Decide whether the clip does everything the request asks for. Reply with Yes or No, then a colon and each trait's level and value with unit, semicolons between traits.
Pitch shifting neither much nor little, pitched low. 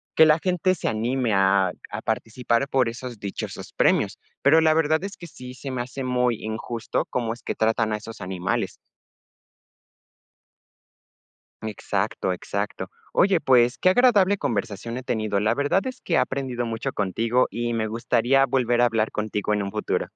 Yes: average, 3.9 semitones; low, 120 Hz